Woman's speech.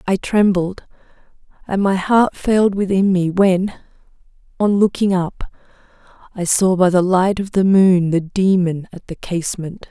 Yes: female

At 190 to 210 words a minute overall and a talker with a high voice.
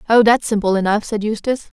Yes: average, 200 wpm; high, 215 Hz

